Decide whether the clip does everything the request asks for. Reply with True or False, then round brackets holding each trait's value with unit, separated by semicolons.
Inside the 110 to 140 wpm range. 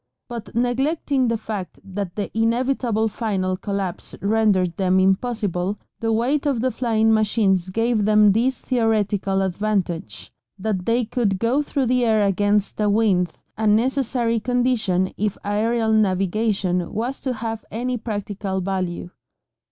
True (135 wpm)